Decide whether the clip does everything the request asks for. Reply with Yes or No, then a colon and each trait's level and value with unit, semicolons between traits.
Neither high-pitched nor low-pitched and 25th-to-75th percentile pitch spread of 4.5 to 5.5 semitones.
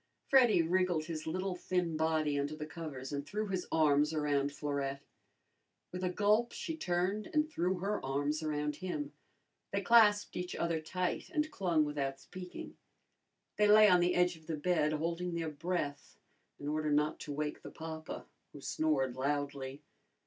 No: medium, 160 Hz; average, 3.7 semitones